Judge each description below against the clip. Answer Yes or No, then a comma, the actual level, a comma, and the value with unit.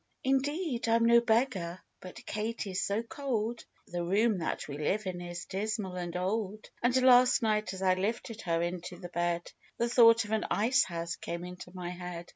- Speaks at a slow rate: No, average, 195 wpm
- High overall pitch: Yes, high, 200 Hz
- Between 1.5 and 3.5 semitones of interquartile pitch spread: No, average, 4.6 semitones